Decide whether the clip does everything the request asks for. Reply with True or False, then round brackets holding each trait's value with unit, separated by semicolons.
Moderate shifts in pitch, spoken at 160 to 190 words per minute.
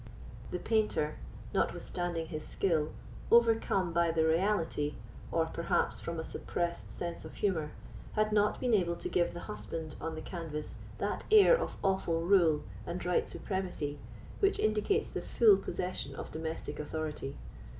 False (3.8 semitones; 150 wpm)